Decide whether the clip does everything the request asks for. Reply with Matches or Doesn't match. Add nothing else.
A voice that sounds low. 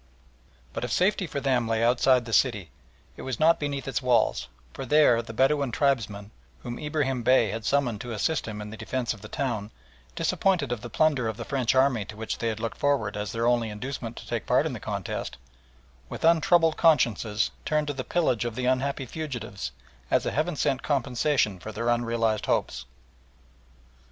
Matches